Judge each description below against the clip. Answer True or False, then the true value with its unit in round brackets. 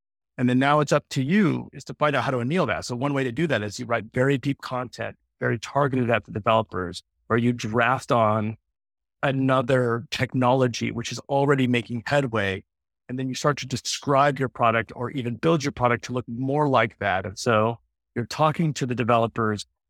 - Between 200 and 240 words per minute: True (205 wpm)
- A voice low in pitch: True (125 Hz)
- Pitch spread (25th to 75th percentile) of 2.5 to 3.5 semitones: True (3.2 semitones)